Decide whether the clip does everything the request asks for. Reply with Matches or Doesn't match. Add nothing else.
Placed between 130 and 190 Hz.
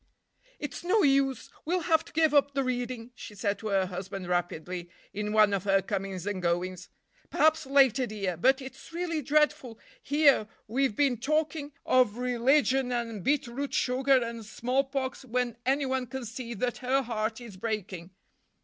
Doesn't match